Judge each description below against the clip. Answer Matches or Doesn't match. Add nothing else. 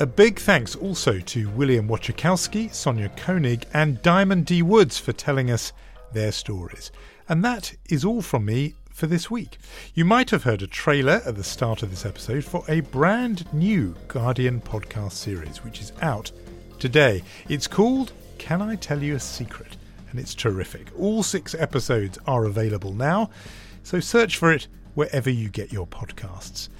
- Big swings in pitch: Matches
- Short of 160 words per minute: Doesn't match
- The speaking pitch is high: Doesn't match